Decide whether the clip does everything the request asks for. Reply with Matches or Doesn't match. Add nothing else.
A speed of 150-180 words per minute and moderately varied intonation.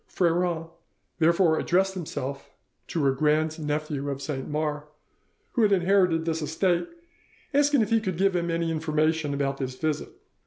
Matches